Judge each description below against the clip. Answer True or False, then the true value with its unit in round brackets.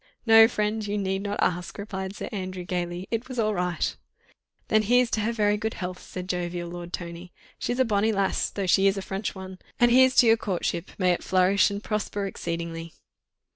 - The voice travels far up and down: False (3.1 semitones)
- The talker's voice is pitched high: True (195 Hz)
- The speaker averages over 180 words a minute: True (200 wpm)